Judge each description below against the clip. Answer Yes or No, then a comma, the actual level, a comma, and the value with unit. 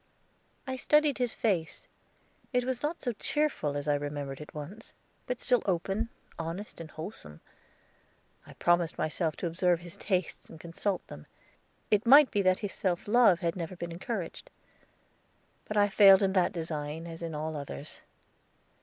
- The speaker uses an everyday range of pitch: Yes, average, 4.8 semitones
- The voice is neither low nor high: Yes, medium, 180 Hz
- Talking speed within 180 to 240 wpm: No, average, 165 wpm